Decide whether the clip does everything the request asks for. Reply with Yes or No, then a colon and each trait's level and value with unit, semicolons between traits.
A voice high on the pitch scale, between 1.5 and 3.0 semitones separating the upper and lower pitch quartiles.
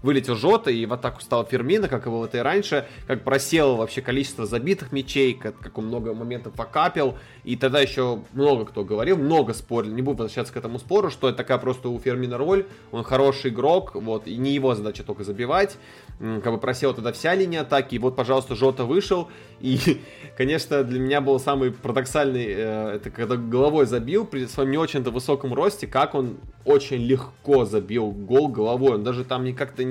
No: low, 130 Hz; narrow, 2.6 semitones